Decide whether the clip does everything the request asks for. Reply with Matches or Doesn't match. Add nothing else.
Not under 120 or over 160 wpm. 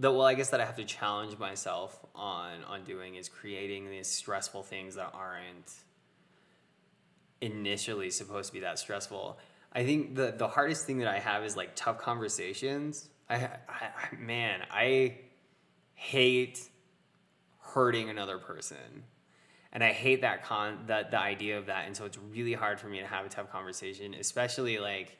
Doesn't match